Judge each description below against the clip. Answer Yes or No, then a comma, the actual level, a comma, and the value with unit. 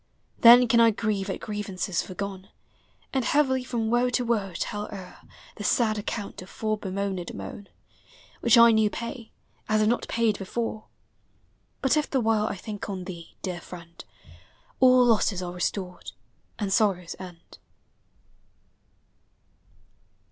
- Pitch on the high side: Yes, high, 210 Hz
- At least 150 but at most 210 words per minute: No, average, 140 wpm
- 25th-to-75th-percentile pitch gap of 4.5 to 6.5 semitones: No, average, 3.7 semitones